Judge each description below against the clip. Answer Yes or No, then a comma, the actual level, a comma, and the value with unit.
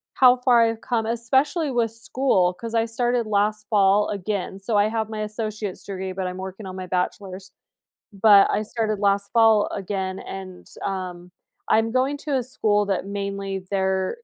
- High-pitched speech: Yes, high, 210 Hz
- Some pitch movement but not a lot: Yes, average, 3.0 semitones